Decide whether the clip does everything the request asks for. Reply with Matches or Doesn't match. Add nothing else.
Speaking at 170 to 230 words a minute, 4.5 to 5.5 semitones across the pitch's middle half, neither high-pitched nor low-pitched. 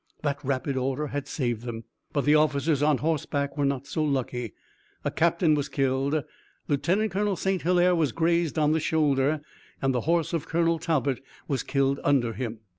Doesn't match